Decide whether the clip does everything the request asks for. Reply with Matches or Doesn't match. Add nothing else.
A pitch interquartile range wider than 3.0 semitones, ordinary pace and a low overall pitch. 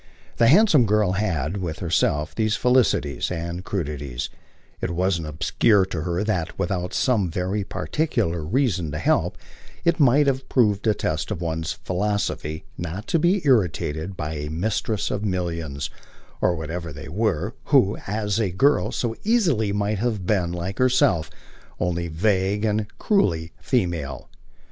Matches